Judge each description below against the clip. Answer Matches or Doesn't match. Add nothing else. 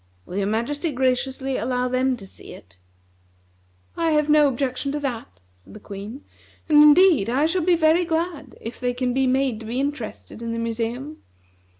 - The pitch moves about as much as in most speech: Matches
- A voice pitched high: Matches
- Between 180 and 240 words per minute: Matches